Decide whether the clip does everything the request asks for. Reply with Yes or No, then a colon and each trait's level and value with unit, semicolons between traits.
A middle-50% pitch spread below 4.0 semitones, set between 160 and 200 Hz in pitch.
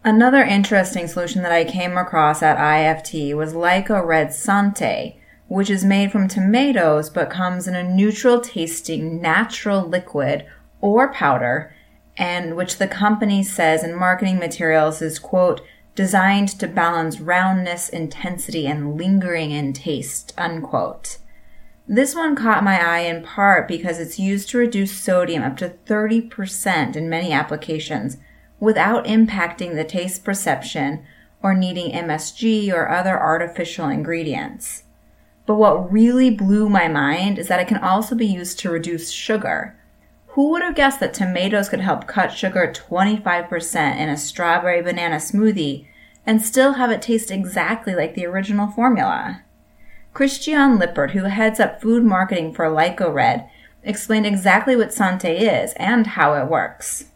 No: average, 4.3 semitones; medium, 185 Hz